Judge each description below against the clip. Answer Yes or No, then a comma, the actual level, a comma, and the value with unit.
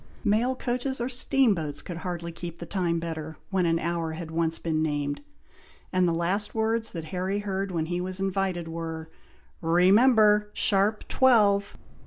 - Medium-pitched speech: Yes, medium, 180 Hz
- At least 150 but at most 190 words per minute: Yes, average, 160 wpm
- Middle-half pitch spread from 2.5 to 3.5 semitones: No, average, 4.0 semitones